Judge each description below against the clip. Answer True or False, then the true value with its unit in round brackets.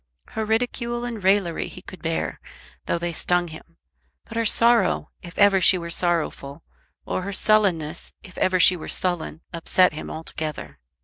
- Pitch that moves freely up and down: False (4.0 semitones)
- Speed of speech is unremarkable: True (165 wpm)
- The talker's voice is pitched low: False (180 Hz)